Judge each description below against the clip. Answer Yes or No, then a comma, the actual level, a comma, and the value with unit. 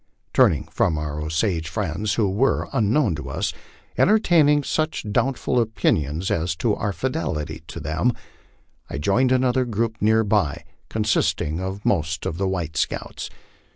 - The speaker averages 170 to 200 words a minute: No, average, 145 wpm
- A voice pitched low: Yes, low, 100 Hz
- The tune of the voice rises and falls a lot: Yes, wide, 7.1 semitones